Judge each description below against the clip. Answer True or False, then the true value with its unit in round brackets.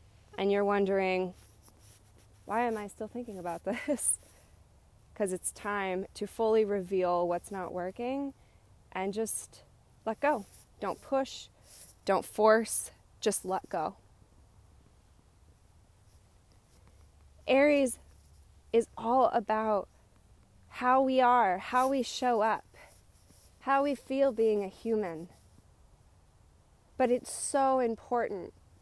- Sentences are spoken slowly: True (105 wpm)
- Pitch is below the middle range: False (195 Hz)